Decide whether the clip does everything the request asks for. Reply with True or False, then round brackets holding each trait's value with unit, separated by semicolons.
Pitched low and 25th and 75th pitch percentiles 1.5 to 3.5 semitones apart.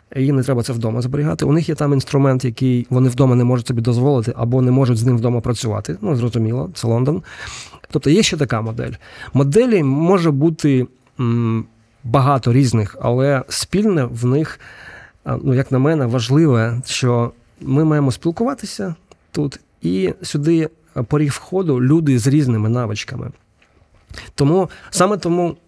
False (130 Hz; 4.1 semitones)